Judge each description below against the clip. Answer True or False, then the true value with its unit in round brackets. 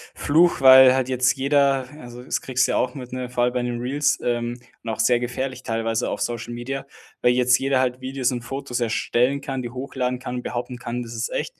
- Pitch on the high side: False (125 Hz)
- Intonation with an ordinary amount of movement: False (1.5 semitones)